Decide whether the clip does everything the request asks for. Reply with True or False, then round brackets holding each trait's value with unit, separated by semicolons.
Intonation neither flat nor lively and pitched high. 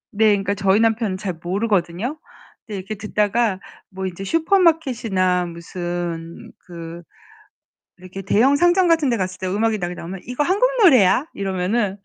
True (4.6 semitones; 200 Hz)